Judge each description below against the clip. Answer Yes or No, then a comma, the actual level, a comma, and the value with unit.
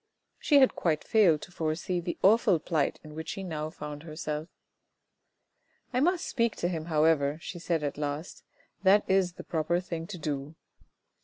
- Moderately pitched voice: Yes, medium, 165 Hz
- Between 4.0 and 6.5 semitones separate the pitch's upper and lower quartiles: No, average, 3.5 semitones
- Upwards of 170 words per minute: Yes, average, 180 wpm